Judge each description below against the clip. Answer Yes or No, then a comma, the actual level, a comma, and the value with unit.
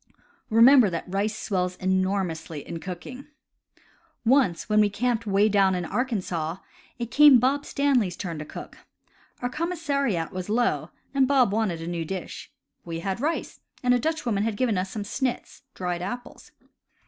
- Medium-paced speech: Yes, average, 160 wpm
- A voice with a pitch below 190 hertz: No, high, 210 Hz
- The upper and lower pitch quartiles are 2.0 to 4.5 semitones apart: No, wide, 5.5 semitones